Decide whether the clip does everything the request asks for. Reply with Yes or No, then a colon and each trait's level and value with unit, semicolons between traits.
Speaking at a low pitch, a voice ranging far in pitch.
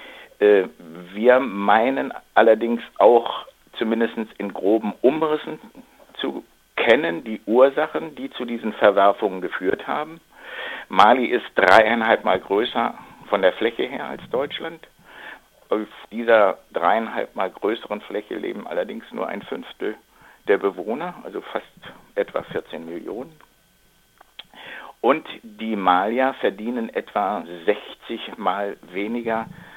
Yes: low, 120 Hz; wide, 7.3 semitones